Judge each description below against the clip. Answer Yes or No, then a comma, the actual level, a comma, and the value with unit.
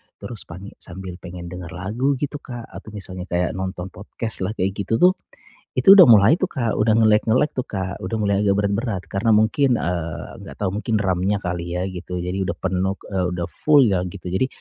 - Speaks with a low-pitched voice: Yes, low, 100 Hz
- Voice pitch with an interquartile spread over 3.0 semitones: Yes, average, 3.7 semitones